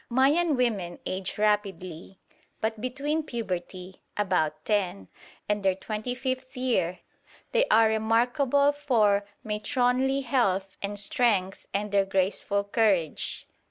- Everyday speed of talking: No, slow, 115 wpm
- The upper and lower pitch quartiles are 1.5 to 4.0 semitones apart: No, average, 4.7 semitones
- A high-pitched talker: Yes, high, 210 Hz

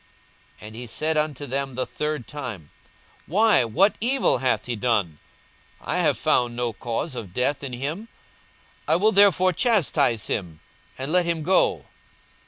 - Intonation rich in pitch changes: Yes, wide, 6.2 semitones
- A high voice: No, medium, 140 Hz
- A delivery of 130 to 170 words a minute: Yes, average, 160 wpm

